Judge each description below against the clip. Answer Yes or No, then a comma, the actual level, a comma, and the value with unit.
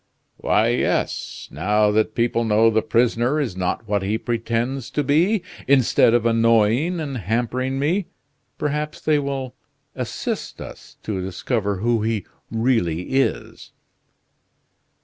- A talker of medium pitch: No, low, 115 Hz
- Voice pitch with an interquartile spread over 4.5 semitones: No, average, 3.8 semitones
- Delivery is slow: Yes, slow, 130 wpm